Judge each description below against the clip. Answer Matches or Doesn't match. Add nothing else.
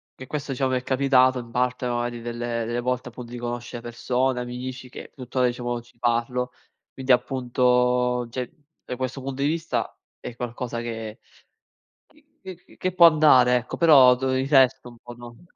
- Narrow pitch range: Matches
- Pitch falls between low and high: Doesn't match